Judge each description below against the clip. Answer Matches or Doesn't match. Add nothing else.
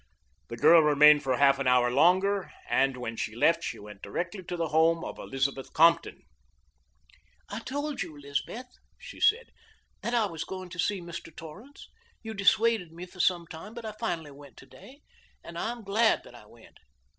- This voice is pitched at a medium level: Matches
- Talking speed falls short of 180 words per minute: Doesn't match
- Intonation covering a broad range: Matches